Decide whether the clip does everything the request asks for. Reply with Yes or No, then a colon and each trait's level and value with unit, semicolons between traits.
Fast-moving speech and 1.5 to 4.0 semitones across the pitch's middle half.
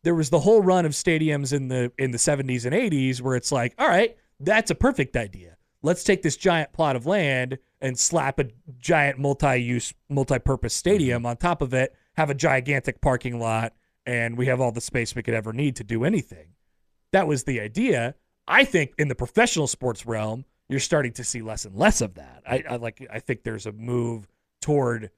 Yes: fast, 210 wpm; average, 3.7 semitones